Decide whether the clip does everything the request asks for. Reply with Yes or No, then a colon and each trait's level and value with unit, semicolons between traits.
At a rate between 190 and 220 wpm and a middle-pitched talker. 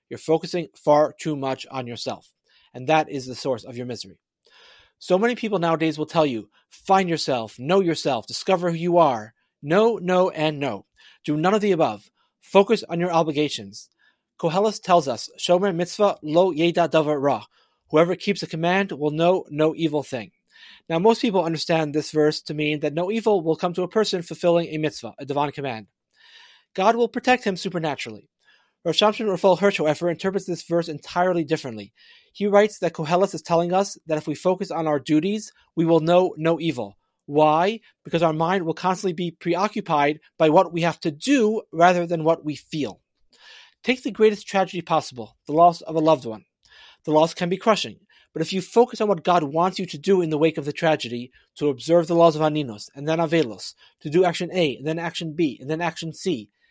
Yes: average, 200 wpm; medium, 165 Hz